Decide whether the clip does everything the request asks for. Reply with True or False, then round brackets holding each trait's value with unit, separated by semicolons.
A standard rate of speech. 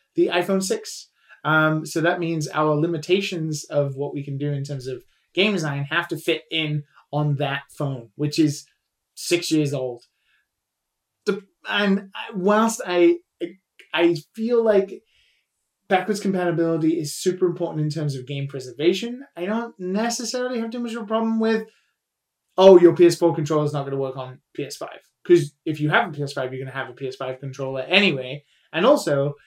True (170 wpm)